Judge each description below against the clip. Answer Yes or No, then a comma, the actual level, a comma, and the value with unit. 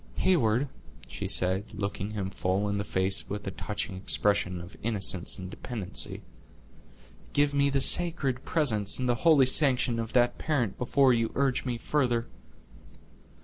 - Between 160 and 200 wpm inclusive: No, average, 150 wpm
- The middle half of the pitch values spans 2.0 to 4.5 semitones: No, average, 5.0 semitones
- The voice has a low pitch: Yes, low, 115 Hz